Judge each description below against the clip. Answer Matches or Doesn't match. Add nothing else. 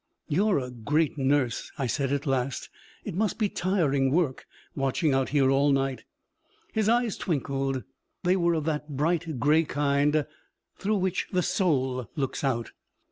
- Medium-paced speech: Matches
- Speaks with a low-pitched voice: Doesn't match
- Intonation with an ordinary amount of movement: Matches